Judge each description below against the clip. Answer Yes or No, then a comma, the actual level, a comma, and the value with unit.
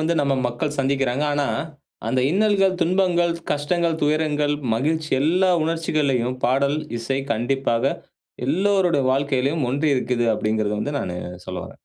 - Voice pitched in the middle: Yes, medium, 145 Hz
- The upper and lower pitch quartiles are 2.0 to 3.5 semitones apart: No, average, 3.9 semitones